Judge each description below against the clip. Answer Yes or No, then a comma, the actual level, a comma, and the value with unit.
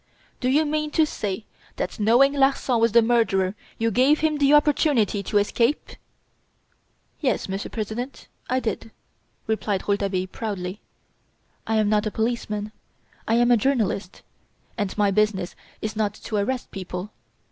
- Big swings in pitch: No, average, 3.9 semitones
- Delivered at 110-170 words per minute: Yes, average, 145 wpm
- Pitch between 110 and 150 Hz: No, high, 220 Hz